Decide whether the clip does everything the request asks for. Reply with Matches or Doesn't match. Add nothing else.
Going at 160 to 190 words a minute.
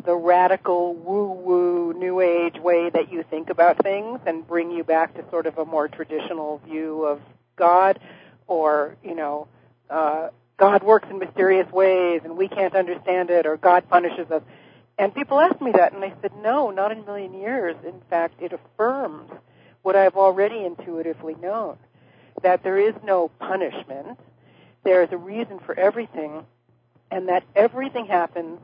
Matches